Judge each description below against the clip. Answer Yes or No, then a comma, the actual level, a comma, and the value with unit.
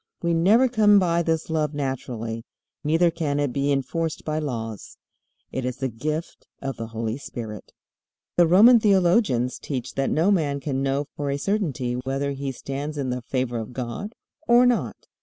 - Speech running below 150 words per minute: No, average, 175 wpm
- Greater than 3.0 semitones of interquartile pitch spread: Yes, average, 4.9 semitones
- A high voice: No, medium, 140 Hz